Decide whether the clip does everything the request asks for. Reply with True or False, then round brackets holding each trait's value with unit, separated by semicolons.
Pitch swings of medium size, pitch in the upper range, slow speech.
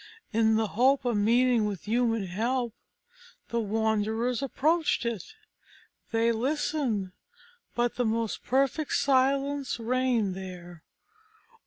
True (3.0 semitones; 235 Hz; 110 wpm)